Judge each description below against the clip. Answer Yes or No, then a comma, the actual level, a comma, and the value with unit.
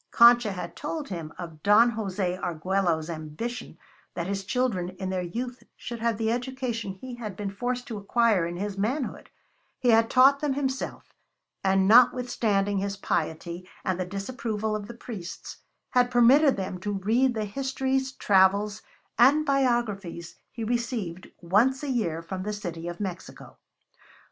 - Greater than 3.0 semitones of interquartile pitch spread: Yes, average, 4.6 semitones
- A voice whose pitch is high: Yes, high, 210 Hz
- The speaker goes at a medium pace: Yes, average, 155 wpm